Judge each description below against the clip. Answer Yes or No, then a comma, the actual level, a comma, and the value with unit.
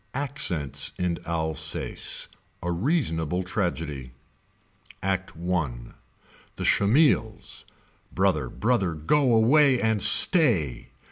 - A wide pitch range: Yes, wide, 7.0 semitones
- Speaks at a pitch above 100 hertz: No, very low, 95 Hz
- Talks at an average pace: No, slow, 85 wpm